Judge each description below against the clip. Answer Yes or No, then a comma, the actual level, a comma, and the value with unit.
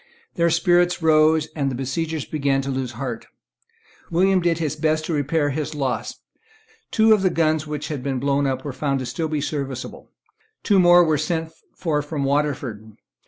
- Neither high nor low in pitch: Yes, medium, 150 Hz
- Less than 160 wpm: No, average, 180 wpm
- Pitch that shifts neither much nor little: Yes, average, 3.0 semitones